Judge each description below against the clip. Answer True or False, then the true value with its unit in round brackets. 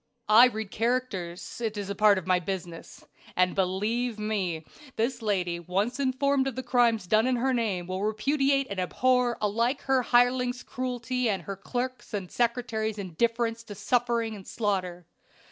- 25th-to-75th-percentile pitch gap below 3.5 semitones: False (4.2 semitones)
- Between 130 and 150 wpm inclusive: False (160 wpm)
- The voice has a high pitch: True (225 Hz)